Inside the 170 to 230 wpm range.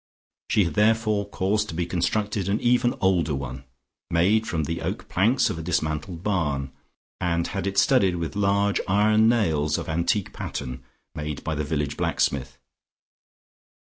No: average, 155 wpm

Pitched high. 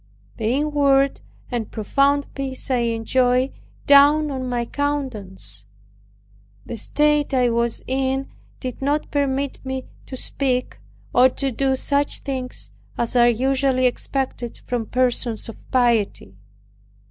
Yes: very high, 260 Hz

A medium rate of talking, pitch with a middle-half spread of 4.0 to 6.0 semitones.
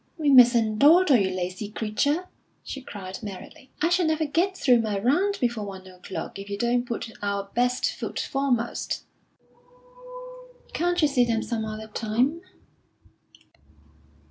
Yes: average, 145 wpm; wide, 5.6 semitones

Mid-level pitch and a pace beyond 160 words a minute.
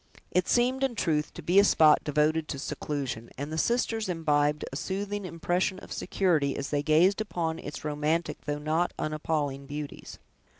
Yes: medium, 155 Hz; average, 170 wpm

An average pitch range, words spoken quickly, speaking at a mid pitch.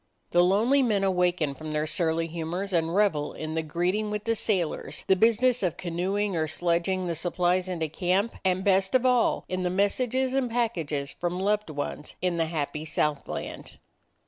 No: average, 4.0 semitones; average, 175 wpm; medium, 180 Hz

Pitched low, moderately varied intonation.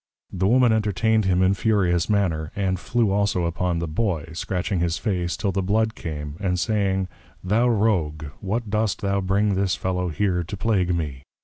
Yes: very low, 95 Hz; average, 3.2 semitones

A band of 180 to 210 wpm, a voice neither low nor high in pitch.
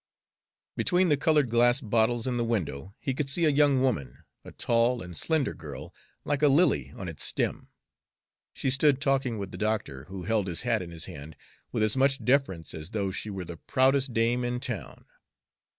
No: average, 195 wpm; low, 115 Hz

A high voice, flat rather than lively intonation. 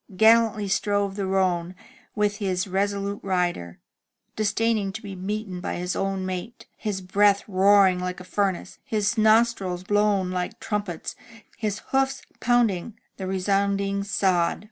Yes: high, 200 Hz; narrow, 2.1 semitones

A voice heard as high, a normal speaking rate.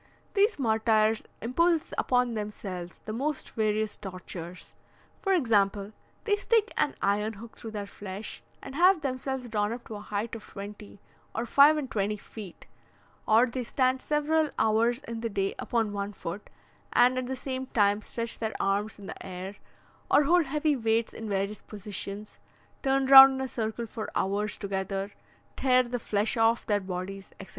Yes: high, 220 Hz; average, 170 wpm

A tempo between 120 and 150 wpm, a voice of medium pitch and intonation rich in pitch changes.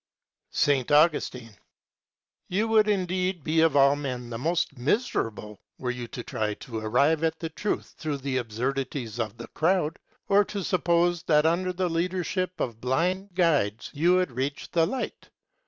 No: average, 160 wpm; medium, 155 Hz; wide, 6.2 semitones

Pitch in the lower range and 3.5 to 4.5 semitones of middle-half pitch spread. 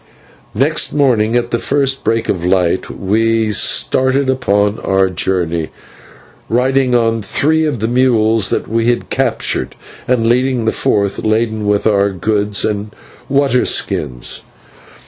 Yes: low, 115 Hz; average, 3.9 semitones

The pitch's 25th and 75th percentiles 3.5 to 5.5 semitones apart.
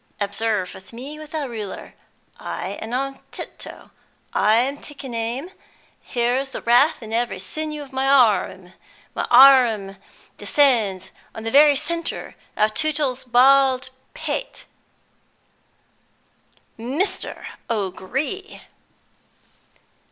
Yes: average, 4.2 semitones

